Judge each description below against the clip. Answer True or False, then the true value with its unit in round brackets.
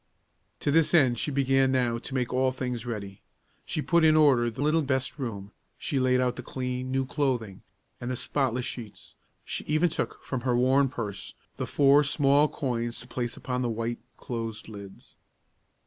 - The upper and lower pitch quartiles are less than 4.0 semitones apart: True (2.6 semitones)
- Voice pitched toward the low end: True (125 Hz)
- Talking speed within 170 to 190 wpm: True (180 wpm)